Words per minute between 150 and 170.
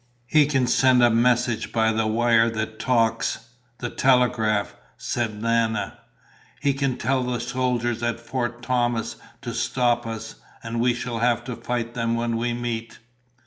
Yes: average, 155 wpm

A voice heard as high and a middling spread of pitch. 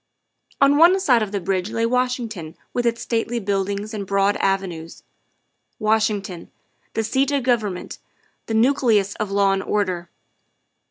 Yes: high, 215 Hz; average, 3.5 semitones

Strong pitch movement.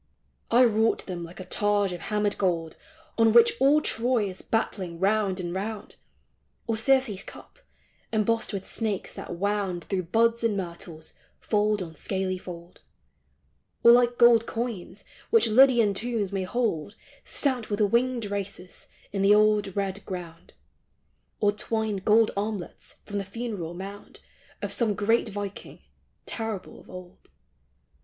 No: average, 3.3 semitones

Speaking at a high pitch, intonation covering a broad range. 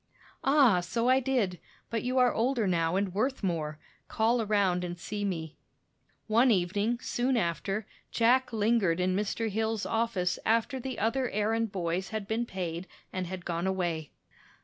No: high, 210 Hz; average, 4.5 semitones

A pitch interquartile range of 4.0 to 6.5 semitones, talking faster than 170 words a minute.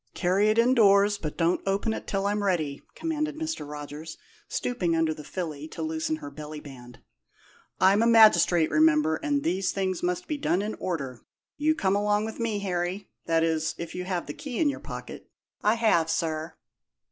Yes: average, 5.0 semitones; average, 185 wpm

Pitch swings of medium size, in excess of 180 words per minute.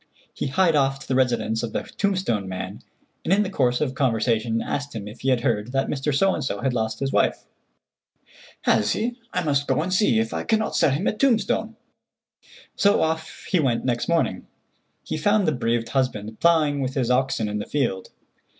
No: wide, 6.2 semitones; average, 195 wpm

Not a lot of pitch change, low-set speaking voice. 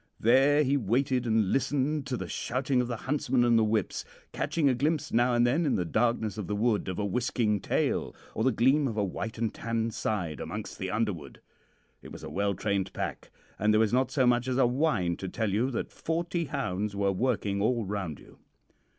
No: average, 4.2 semitones; low, 115 Hz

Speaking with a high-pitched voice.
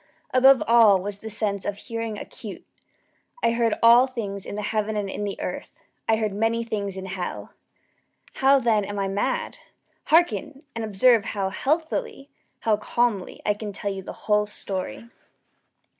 Yes: high, 215 Hz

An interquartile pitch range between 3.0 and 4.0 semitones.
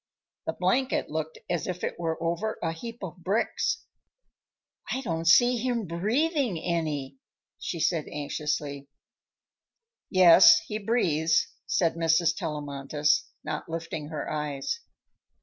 No: average, 4.6 semitones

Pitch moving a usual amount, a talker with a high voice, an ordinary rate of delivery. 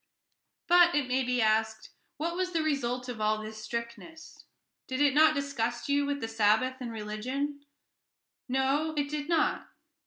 Yes: average, 4.6 semitones; very high, 260 Hz; average, 165 wpm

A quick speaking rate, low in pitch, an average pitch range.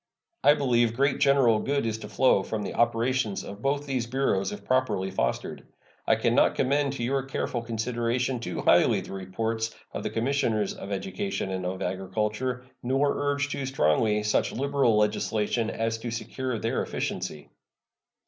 No: average, 165 wpm; low, 115 Hz; average, 4.0 semitones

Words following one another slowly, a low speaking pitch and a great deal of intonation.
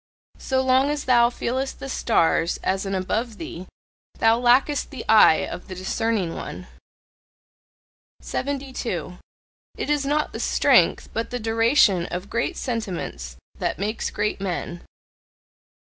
No: slow, 130 wpm; high, 225 Hz; wide, 5.7 semitones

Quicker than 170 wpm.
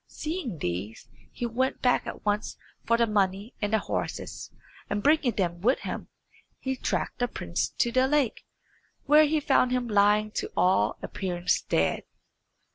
No: average, 160 wpm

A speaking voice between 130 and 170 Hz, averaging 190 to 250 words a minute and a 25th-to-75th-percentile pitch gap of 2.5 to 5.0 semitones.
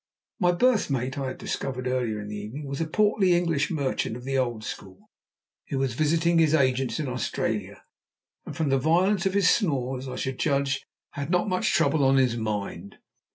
Yes: medium, 140 Hz; average, 195 wpm; average, 4.5 semitones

